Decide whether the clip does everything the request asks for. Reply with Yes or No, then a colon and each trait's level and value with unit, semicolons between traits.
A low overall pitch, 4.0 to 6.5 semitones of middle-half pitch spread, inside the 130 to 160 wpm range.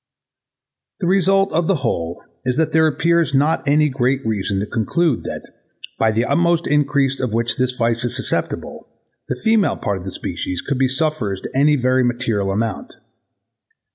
No: low, 130 Hz; wide, 5.5 semitones; average, 170 wpm